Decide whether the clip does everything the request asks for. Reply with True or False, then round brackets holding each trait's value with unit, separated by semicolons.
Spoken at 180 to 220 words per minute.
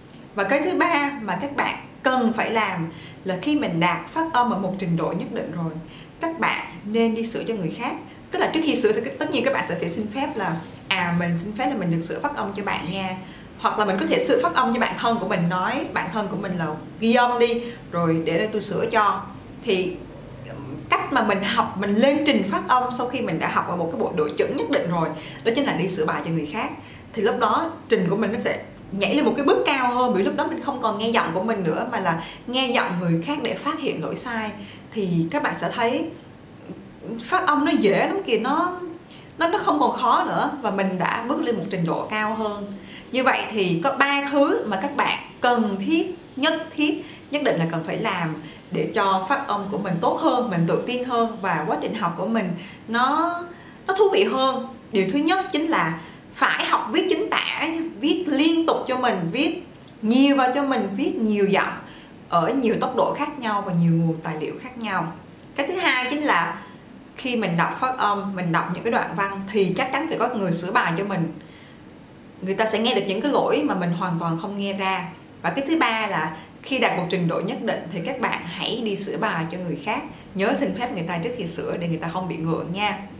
False (245 wpm)